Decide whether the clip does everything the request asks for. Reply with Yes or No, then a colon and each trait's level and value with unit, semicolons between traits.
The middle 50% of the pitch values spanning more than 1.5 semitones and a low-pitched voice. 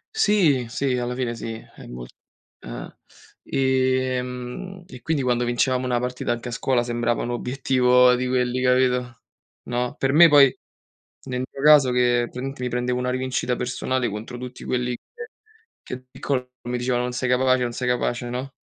No: narrow, 1.0 semitones; low, 125 Hz